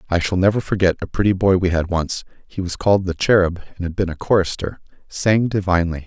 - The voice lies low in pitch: Yes, very low, 90 Hz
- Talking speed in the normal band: No, fast, 210 wpm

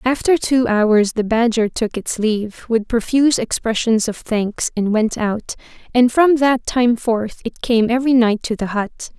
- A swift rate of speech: No, average, 185 wpm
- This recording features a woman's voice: Yes, female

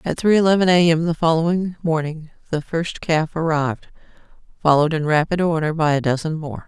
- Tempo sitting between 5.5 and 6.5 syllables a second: Yes, 5.7 syllables/s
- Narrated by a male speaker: No, female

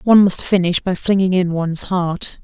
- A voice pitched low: No, medium, 185 Hz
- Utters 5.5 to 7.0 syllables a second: No, 5.2 syllables/s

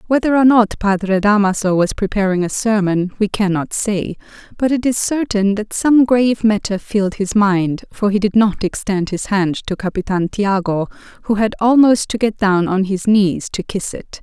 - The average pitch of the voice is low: No, high, 205 Hz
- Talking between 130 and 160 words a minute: No, average, 190 wpm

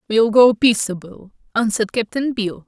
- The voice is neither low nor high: No, high, 220 Hz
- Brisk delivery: No, slow, 135 wpm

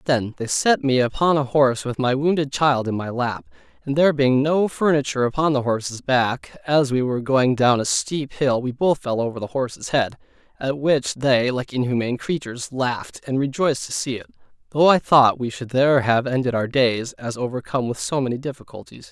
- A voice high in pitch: No, low, 130 Hz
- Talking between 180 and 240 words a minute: Yes, fast, 205 wpm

